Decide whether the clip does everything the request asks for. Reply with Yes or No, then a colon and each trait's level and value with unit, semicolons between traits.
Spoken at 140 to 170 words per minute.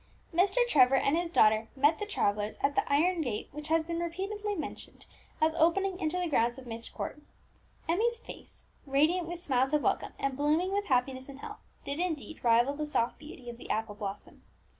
No: average, 195 wpm